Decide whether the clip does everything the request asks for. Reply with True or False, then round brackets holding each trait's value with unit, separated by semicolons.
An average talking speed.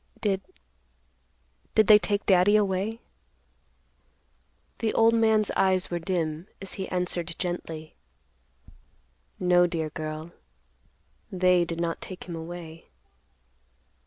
False (100 wpm)